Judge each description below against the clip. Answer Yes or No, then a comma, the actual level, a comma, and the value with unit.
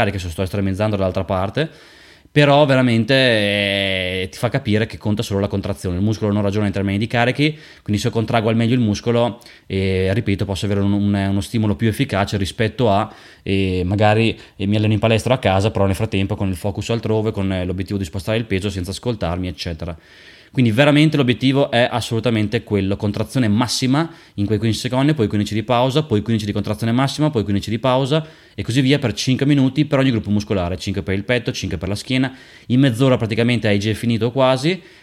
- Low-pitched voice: Yes, low, 110 Hz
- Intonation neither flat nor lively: Yes, average, 3.8 semitones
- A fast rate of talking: Yes, fast, 205 wpm